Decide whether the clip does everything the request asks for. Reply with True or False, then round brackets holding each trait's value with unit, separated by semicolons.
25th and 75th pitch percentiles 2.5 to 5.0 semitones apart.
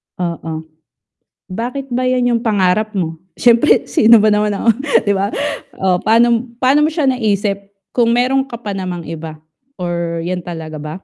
False (5.4 semitones)